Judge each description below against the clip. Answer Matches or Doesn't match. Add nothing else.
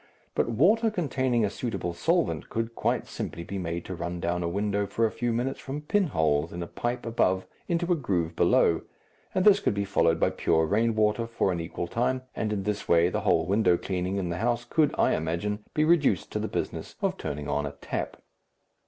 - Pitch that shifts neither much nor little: Doesn't match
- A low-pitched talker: Matches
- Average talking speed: Doesn't match